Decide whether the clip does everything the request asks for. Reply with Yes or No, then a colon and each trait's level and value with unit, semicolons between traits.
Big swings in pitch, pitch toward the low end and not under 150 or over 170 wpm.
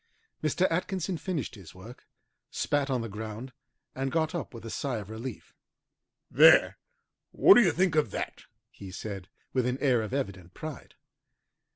Yes: wide, 6.2 semitones; low, 130 Hz; average, 165 wpm